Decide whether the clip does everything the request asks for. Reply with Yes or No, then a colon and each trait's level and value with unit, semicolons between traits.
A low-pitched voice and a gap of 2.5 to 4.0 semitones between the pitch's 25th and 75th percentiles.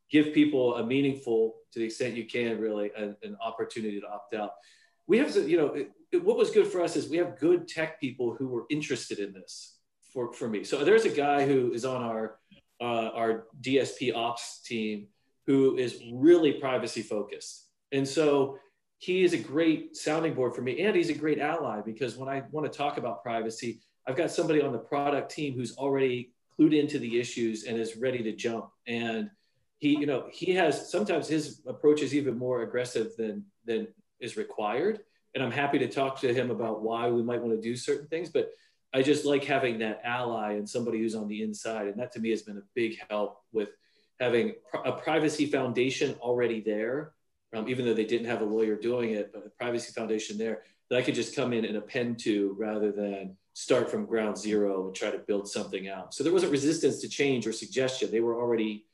No: low, 125 Hz; average, 4.6 semitones